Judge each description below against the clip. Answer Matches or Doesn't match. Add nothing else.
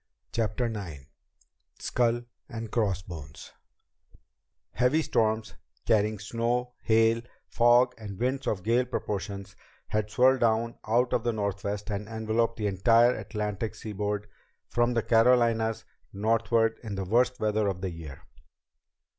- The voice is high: Doesn't match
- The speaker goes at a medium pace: Doesn't match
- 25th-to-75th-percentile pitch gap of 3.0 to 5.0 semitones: Doesn't match